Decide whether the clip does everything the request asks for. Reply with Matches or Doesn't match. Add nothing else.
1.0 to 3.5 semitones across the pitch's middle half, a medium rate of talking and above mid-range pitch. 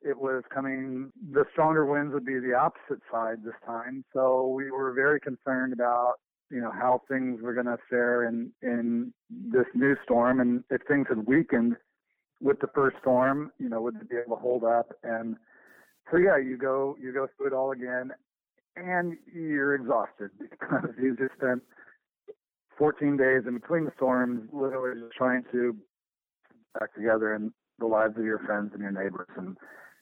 Doesn't match